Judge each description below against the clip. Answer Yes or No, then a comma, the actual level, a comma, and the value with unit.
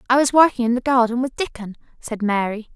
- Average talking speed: No, fast, 220 wpm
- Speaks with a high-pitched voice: Yes, high, 240 Hz